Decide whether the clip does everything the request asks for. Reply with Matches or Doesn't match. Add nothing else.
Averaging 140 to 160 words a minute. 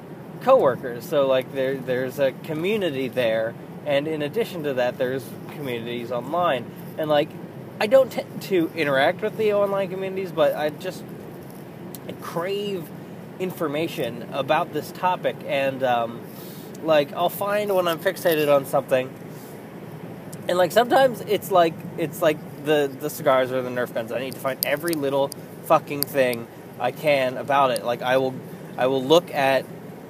Matches